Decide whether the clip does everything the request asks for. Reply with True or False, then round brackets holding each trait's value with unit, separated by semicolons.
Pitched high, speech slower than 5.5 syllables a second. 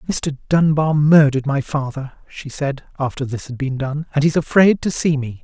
False (145 Hz; 5.0 syllables/s)